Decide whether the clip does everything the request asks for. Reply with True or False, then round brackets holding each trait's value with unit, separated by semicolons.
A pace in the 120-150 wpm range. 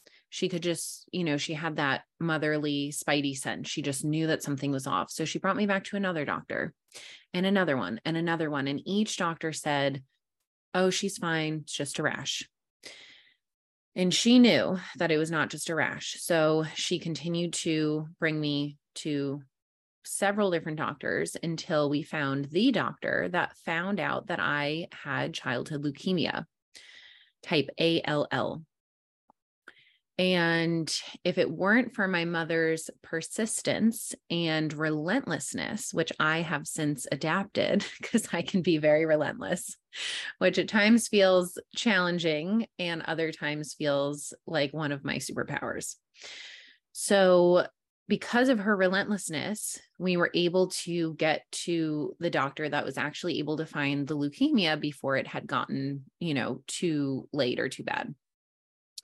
True (145 wpm)